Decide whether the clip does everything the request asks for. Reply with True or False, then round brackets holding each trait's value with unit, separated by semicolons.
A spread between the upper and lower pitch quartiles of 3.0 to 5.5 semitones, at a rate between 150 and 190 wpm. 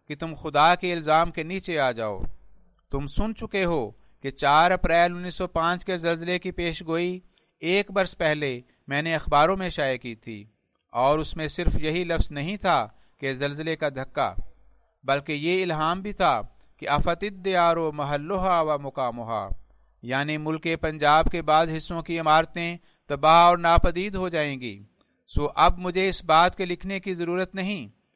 True (3.5 semitones; 175 wpm)